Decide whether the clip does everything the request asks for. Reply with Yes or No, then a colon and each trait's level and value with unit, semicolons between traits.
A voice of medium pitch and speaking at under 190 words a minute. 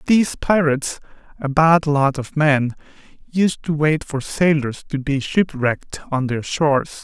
Yes: medium, 150 Hz; average, 155 wpm